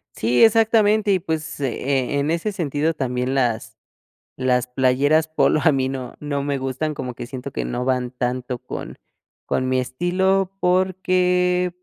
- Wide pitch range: Yes, wide, 5.9 semitones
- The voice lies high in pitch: No, medium, 140 Hz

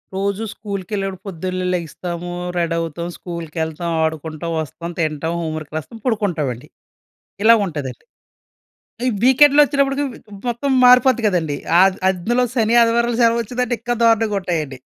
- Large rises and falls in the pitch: Yes, wide, 6.0 semitones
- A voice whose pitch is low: No, high, 190 Hz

